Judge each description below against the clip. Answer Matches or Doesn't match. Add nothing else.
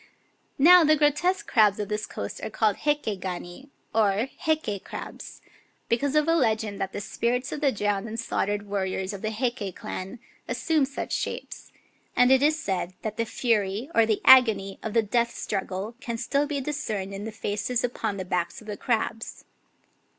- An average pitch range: Matches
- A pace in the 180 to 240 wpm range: Matches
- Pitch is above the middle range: Matches